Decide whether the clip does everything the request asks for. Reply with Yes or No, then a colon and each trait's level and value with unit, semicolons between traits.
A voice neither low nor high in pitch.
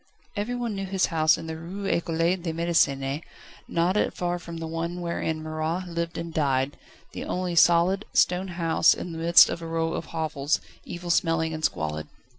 Yes: medium, 165 Hz